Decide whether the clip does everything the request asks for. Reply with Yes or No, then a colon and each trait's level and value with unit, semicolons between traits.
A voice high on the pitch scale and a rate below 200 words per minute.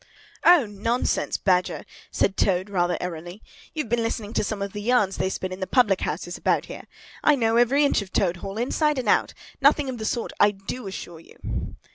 No: high, 210 Hz; fast, 205 wpm